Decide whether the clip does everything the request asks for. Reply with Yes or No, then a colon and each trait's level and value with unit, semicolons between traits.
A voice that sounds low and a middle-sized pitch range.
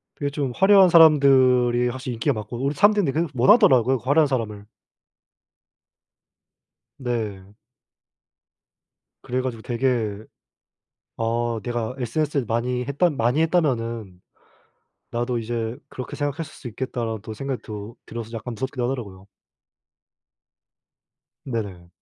Yes: low, 125 Hz; average, 3.4 semitones